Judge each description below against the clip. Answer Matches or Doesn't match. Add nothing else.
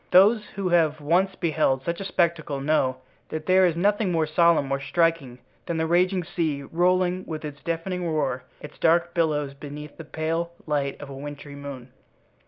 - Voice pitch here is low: Doesn't match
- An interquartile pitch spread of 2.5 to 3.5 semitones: Matches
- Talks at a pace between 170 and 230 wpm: Matches